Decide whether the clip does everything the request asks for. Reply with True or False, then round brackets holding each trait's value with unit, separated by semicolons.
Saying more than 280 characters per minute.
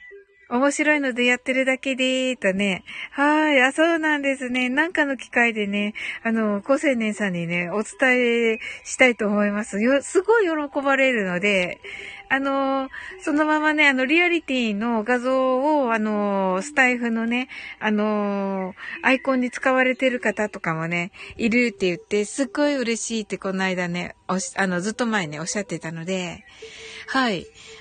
True (315 characters per minute)